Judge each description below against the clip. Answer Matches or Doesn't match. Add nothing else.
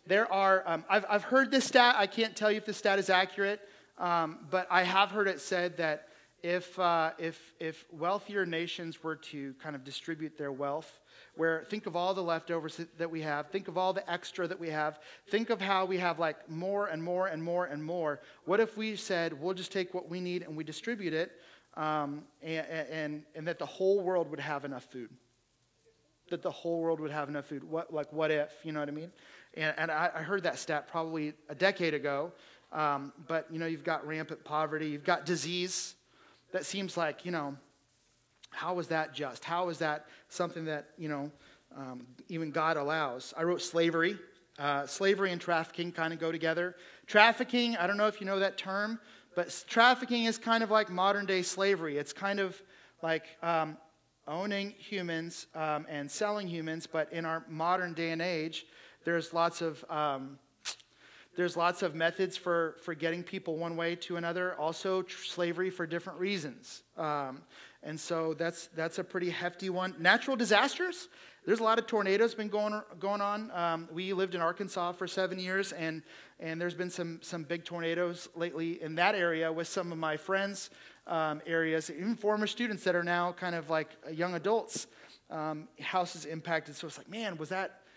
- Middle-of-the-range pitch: Matches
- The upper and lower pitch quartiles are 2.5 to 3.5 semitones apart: Matches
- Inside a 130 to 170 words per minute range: Doesn't match